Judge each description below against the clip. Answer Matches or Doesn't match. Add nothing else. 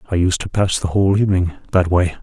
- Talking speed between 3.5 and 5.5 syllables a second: Doesn't match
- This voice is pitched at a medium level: Doesn't match